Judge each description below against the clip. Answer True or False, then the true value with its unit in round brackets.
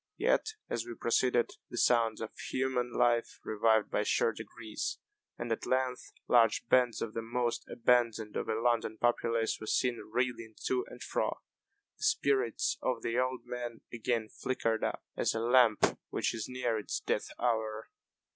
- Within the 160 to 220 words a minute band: True (165 wpm)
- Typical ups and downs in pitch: False (1.8 semitones)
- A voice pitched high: False (120 Hz)